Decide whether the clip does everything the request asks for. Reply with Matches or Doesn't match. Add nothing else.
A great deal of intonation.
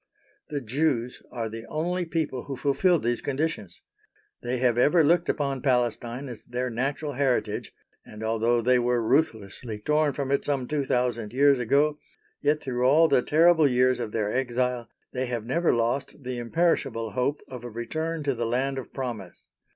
Doesn't match